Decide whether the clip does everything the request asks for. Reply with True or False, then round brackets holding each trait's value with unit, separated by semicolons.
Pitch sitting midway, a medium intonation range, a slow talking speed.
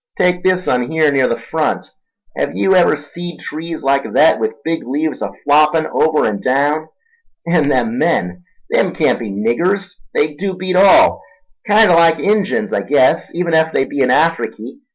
False (155 Hz; 4.5 semitones; 170 wpm)